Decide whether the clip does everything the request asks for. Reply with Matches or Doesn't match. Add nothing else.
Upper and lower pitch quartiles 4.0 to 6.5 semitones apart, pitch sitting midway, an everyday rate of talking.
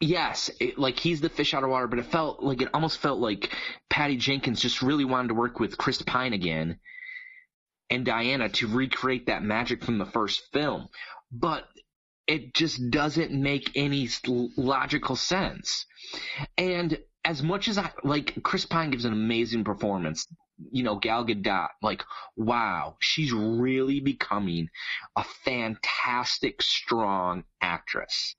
Doesn't match